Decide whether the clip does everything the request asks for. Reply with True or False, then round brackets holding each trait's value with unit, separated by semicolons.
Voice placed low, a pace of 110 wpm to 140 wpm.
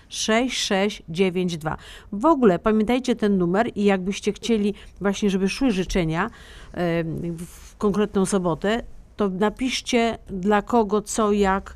False (205 Hz; 115 wpm)